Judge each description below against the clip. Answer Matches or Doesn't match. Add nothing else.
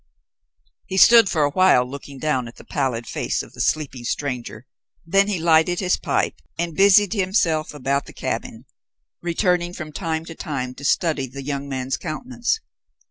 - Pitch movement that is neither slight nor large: Matches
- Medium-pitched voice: Matches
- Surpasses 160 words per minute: Matches